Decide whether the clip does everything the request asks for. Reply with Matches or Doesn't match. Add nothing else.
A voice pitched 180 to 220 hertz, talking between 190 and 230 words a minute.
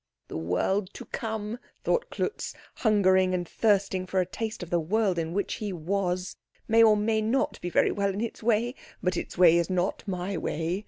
Matches